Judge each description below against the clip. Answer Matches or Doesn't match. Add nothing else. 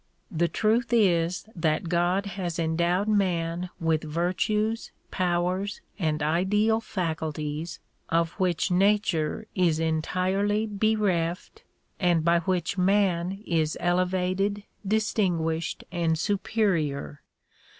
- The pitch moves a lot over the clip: Doesn't match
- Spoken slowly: Matches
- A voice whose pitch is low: Doesn't match